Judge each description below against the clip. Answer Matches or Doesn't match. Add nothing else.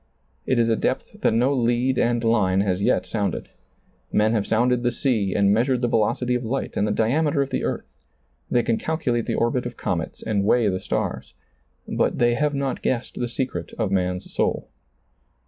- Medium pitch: Doesn't match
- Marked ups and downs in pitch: Doesn't match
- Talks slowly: Doesn't match